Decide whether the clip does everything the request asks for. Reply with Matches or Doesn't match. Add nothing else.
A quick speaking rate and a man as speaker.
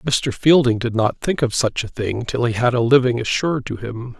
Matches